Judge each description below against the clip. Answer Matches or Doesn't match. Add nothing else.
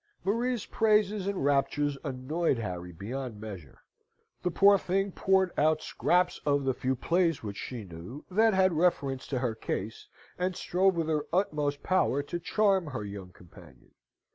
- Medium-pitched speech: Matches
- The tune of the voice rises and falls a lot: Matches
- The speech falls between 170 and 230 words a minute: Doesn't match